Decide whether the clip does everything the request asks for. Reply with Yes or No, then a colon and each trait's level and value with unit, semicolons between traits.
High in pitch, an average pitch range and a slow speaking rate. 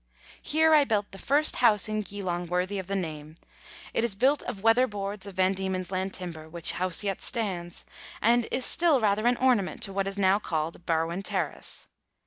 No: high, 195 Hz; average, 3.8 semitones; average, 190 wpm